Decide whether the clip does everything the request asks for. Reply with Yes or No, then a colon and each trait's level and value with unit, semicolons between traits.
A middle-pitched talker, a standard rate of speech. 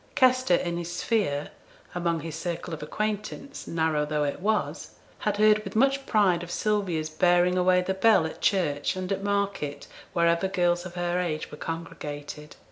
Yes: medium, 175 Hz; average, 170 wpm